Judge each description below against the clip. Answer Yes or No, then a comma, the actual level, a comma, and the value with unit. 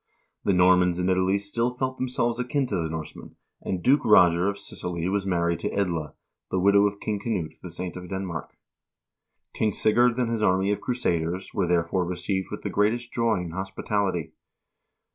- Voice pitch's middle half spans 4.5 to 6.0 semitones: No, average, 3.4 semitones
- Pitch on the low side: Yes, very low, 95 Hz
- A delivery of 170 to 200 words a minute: Yes, average, 180 wpm